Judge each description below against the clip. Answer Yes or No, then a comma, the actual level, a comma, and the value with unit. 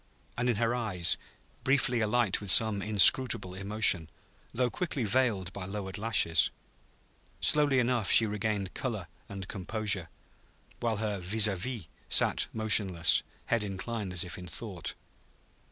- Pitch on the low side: Yes, low, 105 Hz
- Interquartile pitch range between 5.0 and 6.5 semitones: No, average, 3.7 semitones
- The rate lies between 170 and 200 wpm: No, slow, 135 wpm